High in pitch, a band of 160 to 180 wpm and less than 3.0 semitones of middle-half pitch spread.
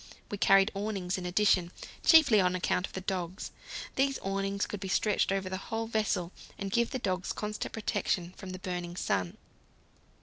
Yes: high, 195 Hz; average, 175 wpm; narrow, 2.5 semitones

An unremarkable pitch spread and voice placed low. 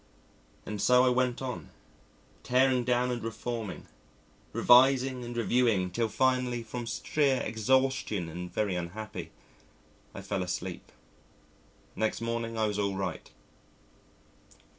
Yes: average, 3.2 semitones; low, 115 Hz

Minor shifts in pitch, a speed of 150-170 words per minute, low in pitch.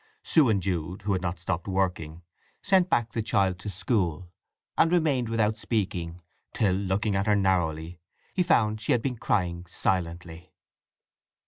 No: average, 4.0 semitones; average, 155 wpm; very low, 95 Hz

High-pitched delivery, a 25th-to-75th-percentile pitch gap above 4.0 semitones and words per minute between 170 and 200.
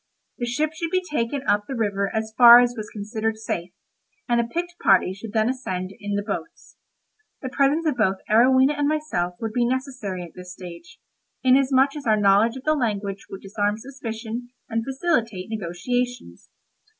Yes: high, 230 Hz; average, 4.4 semitones; average, 175 wpm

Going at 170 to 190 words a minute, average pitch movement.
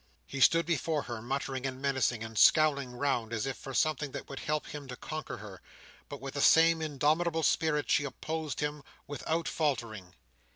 Yes: average, 180 wpm; average, 3.4 semitones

